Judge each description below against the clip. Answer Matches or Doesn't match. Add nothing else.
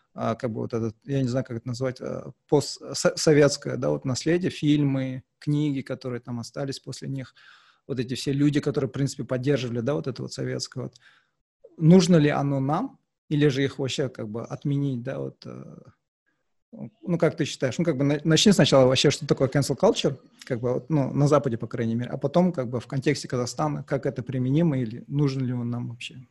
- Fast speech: Matches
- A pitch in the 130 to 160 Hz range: Matches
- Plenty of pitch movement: Doesn't match